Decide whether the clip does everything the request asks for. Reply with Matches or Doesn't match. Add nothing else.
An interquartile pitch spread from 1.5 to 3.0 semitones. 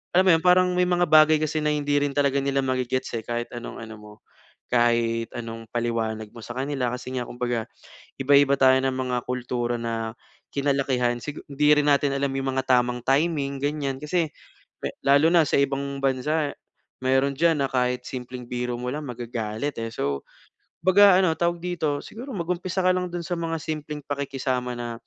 Doesn't match